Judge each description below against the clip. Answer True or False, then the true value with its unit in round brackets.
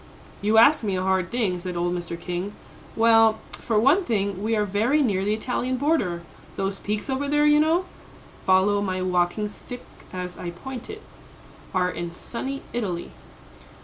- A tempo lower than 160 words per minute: False (170 wpm)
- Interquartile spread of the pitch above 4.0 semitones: True (5.1 semitones)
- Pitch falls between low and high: False (210 Hz)